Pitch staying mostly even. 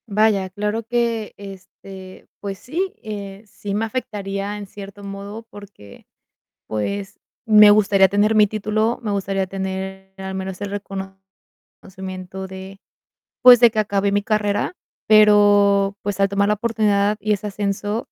Yes: narrow, 1.6 semitones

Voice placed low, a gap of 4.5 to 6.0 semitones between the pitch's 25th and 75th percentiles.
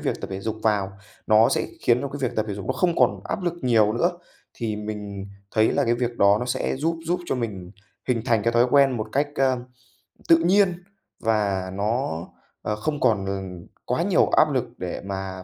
Yes: low, 115 Hz; average, 5.1 semitones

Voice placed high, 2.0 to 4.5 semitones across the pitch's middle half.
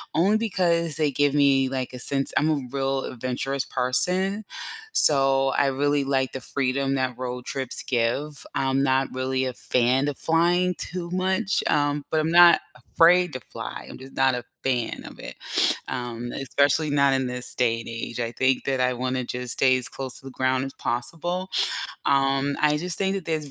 No: low, 135 Hz; average, 3.2 semitones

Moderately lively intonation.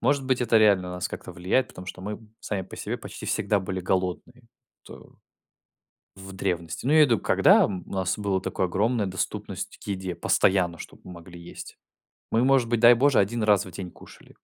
Yes: average, 4.1 semitones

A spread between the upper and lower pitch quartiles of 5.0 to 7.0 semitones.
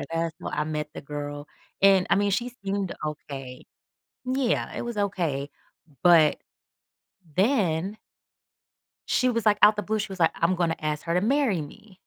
Yes: wide, 5.4 semitones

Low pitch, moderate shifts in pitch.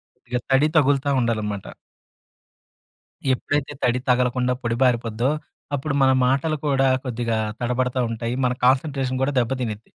No: low, 125 Hz; narrow, 2.2 semitones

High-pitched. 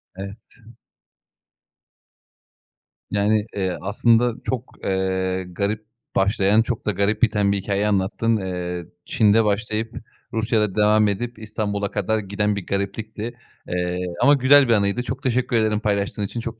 No: low, 105 Hz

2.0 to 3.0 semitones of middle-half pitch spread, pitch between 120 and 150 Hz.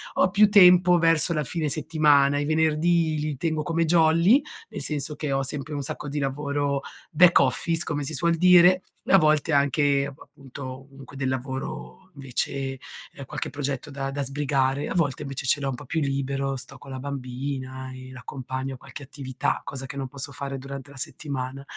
Yes: narrow, 2.6 semitones; medium, 140 Hz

